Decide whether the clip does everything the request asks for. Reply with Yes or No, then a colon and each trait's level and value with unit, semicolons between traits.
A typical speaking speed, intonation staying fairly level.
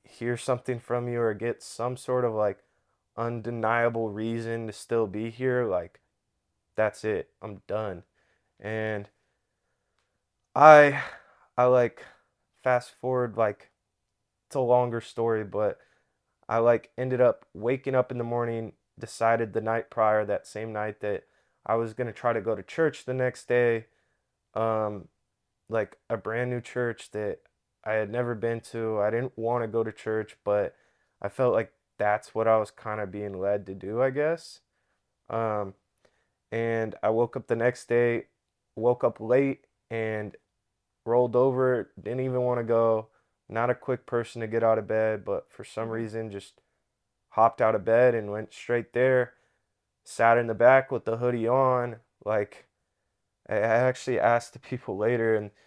Yes: average, 165 wpm; narrow, 2.1 semitones